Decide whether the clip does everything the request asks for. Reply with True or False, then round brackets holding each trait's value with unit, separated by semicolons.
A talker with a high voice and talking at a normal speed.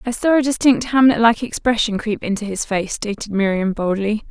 True (220 Hz; 195 wpm)